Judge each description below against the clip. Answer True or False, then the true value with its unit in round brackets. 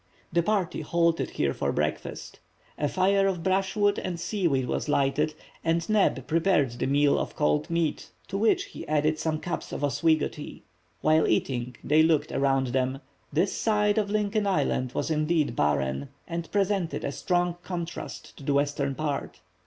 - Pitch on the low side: False (160 Hz)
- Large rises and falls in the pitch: False (5.0 semitones)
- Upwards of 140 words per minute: True (165 wpm)